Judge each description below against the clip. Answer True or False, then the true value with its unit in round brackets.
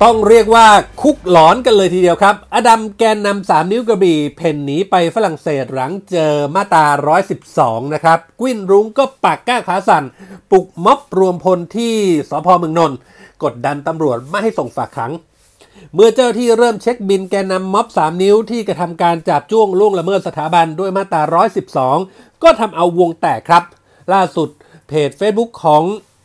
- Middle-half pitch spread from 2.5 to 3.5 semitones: False (4.8 semitones)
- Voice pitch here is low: False (185 Hz)